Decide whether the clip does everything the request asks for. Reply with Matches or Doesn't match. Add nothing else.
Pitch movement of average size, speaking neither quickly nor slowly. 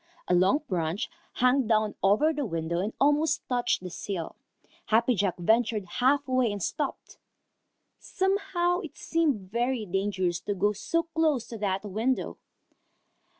Doesn't match